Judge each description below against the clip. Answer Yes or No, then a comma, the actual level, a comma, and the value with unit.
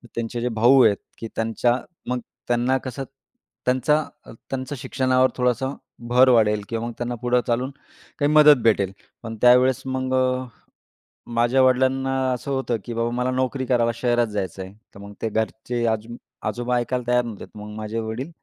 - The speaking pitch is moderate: No, low, 125 Hz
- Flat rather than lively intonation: Yes, narrow, 2.3 semitones